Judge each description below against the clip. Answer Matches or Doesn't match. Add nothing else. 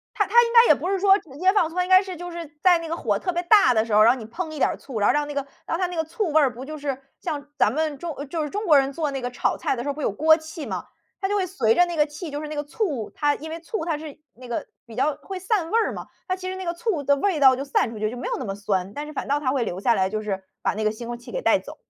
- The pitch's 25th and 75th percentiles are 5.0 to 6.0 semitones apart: Matches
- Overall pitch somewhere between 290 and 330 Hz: Matches